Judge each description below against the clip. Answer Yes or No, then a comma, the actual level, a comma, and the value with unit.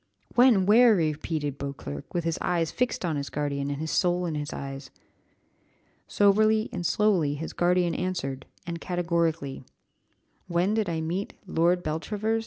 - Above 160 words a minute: No, average, 150 wpm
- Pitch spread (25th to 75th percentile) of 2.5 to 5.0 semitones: Yes, average, 4.4 semitones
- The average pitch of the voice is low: No, medium, 170 Hz